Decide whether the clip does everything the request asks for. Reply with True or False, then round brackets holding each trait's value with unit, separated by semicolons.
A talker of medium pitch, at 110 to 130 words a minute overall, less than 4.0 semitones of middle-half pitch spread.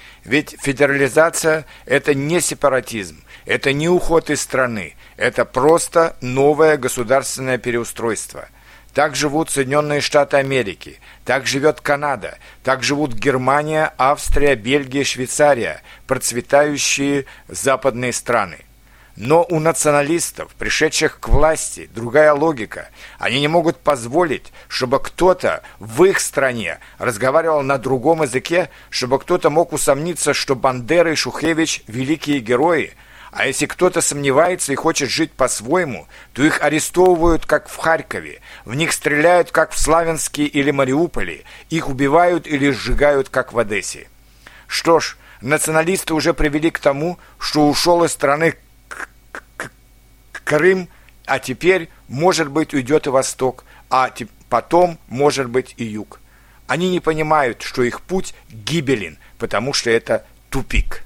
True (145 Hz; 125 wpm; 3.6 semitones)